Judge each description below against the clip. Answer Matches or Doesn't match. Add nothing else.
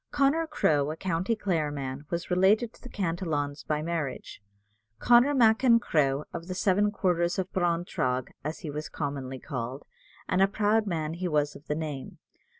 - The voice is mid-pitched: Matches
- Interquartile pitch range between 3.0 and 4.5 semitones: Doesn't match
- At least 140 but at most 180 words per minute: Matches